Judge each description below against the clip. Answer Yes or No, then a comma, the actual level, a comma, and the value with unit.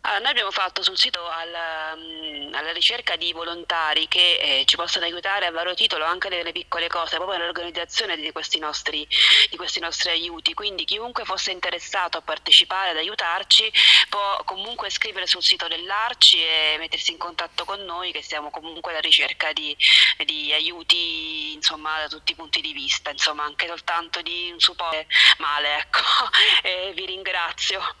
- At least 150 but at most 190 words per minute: Yes, average, 165 wpm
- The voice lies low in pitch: No, medium, 170 Hz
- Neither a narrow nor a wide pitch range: No, narrow, 1.8 semitones